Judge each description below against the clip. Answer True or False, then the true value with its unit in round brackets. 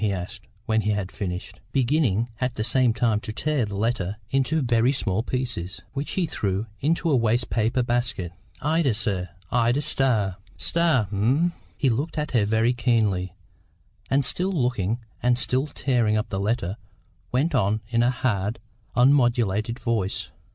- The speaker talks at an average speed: True (160 wpm)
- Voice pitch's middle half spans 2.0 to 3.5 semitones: False (3.9 semitones)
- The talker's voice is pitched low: True (120 Hz)